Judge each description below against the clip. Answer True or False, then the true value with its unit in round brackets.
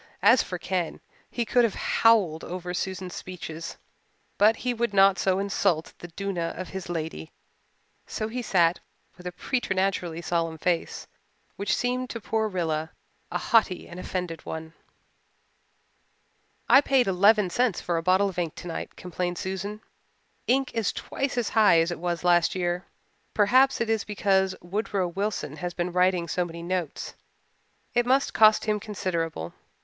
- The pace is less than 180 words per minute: True (155 wpm)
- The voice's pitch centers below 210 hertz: True (185 Hz)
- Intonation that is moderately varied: True (3.7 semitones)